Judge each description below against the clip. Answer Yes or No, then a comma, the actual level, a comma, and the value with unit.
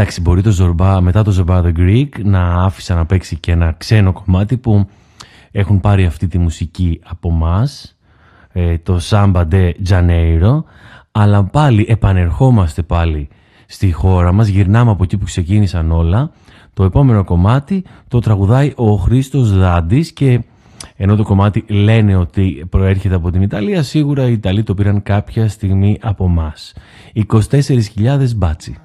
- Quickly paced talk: No, average, 150 wpm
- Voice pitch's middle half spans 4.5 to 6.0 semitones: No, average, 3.6 semitones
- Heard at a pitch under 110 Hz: Yes, low, 100 Hz